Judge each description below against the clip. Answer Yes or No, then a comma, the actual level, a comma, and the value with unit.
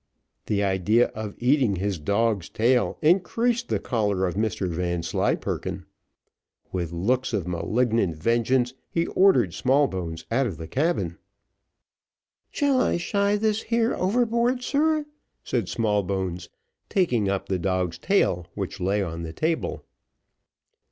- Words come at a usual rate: No, slow, 125 wpm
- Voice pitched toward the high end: No, low, 110 Hz